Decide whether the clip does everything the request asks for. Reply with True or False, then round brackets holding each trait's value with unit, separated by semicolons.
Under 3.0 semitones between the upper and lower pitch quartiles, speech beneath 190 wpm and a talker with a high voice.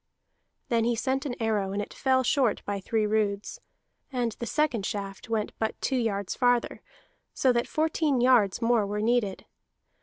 False (3.4 semitones; 170 wpm; 230 Hz)